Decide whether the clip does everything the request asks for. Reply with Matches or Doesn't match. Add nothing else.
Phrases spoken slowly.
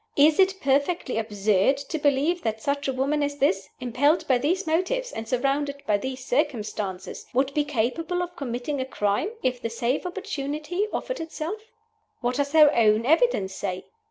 Doesn't match